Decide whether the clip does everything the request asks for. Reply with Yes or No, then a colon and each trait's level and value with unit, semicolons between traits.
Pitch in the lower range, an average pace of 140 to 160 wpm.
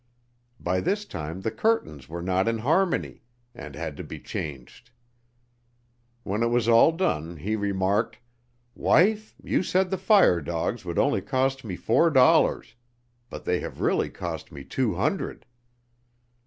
Yes: low, 110 Hz; average, 150 wpm